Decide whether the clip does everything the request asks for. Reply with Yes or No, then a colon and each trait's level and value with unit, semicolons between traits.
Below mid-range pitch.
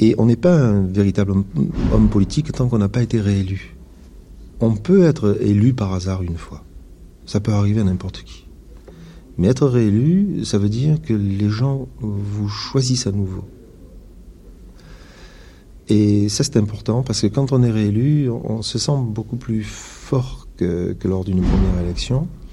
Yes: low, 105 Hz